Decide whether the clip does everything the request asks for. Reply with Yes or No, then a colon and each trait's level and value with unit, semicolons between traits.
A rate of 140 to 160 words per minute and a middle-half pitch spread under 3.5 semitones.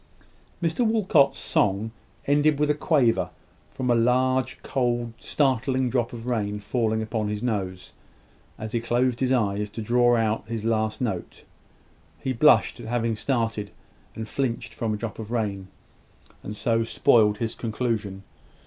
Yes: average, 150 wpm; average, 2.8 semitones